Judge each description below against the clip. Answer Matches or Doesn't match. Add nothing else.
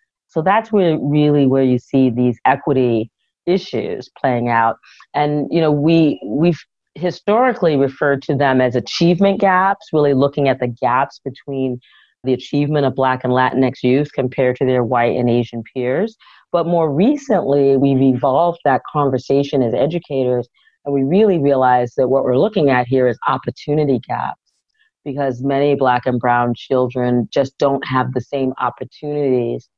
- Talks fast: Doesn't match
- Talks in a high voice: Doesn't match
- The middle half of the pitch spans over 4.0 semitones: Doesn't match